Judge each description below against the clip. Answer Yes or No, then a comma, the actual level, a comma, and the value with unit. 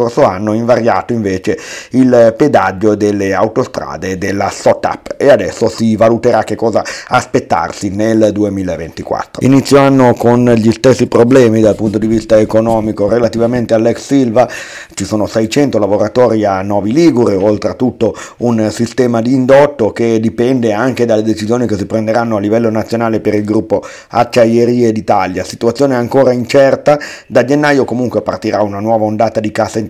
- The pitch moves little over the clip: Yes, narrow, 2.3 semitones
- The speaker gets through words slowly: No, average, 145 wpm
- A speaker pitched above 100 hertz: Yes, low, 115 Hz